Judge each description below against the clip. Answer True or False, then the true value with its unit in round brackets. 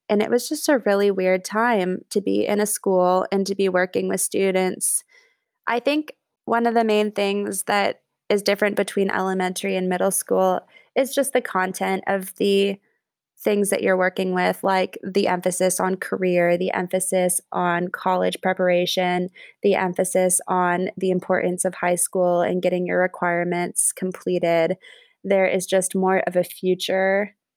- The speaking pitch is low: False (185 Hz)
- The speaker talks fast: False (165 wpm)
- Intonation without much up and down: True (1.8 semitones)